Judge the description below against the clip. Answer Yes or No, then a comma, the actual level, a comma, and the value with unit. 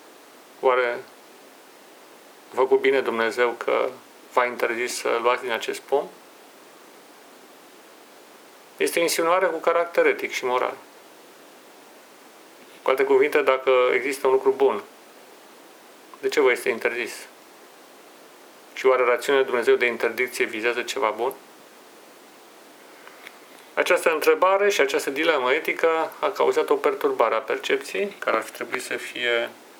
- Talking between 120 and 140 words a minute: Yes, average, 125 wpm